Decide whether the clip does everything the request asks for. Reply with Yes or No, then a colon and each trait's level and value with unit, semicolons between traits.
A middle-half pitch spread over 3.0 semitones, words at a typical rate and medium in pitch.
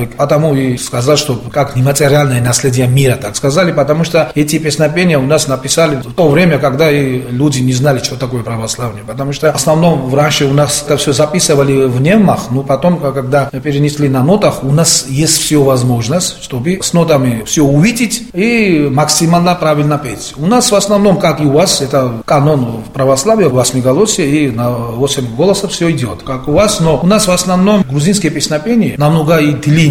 No: average, 3.7 semitones; fast, 190 wpm; medium, 145 Hz